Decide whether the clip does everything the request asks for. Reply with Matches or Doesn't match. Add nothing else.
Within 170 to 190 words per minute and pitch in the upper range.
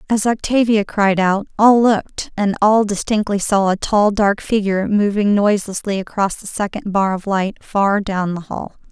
Matches